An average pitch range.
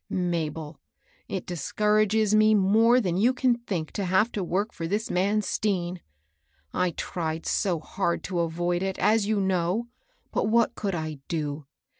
Yes: average, 3.9 semitones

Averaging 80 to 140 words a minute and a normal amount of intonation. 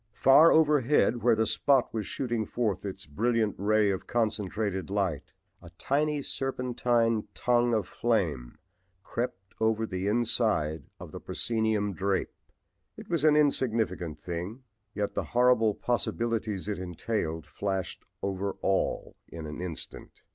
Yes: slow, 135 wpm; average, 4.0 semitones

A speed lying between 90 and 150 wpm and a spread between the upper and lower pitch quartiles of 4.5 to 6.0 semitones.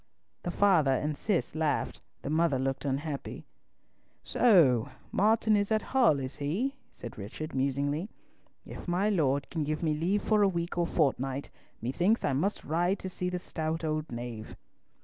No: average, 165 wpm; average, 5.2 semitones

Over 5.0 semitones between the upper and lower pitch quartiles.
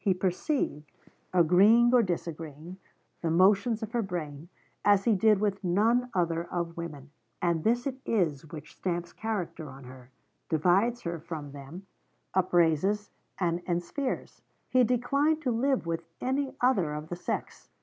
Yes: wide, 5.4 semitones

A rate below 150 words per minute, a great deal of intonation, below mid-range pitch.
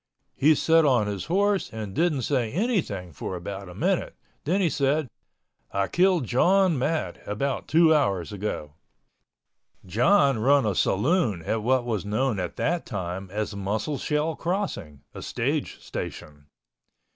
Yes: average, 140 wpm; wide, 8.4 semitones; low, 125 Hz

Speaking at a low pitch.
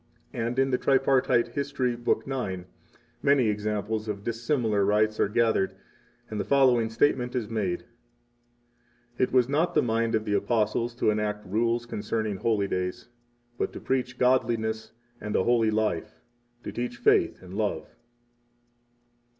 Yes: low, 115 Hz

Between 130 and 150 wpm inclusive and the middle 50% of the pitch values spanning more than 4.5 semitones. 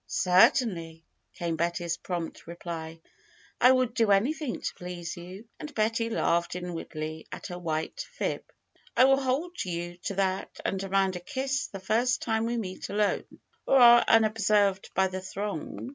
No: average, 160 wpm; average, 5.1 semitones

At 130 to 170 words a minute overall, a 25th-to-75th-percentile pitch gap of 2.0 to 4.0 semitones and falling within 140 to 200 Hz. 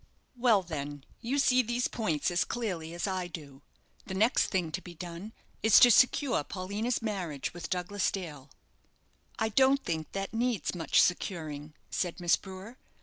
No: average, 160 wpm; average, 5.2 semitones; medium, 185 Hz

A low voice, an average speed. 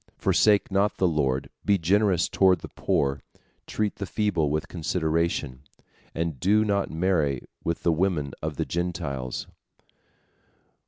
No: very low, 85 Hz; slow, 130 wpm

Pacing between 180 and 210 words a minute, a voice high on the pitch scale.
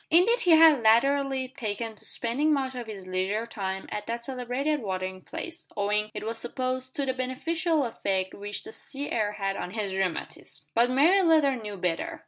Yes: average, 185 wpm; high, 240 Hz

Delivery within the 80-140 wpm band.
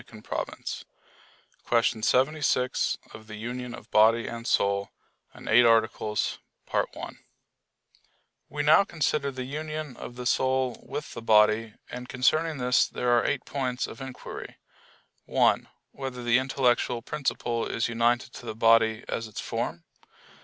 Yes: slow, 135 wpm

